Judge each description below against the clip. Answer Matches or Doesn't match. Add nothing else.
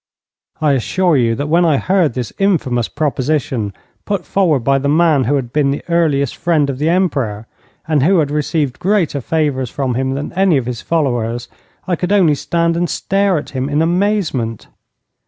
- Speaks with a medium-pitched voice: Matches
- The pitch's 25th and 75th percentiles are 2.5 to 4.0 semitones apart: Doesn't match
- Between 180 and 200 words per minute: Matches